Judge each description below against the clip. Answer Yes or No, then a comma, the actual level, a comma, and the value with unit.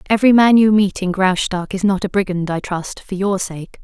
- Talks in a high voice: Yes, high, 195 Hz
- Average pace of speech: No, fast, 235 wpm